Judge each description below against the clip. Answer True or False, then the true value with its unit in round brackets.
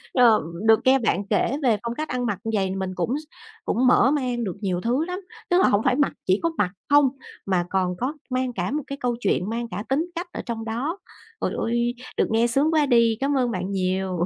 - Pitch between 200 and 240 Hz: True (235 Hz)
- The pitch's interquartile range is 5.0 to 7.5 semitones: True (5.3 semitones)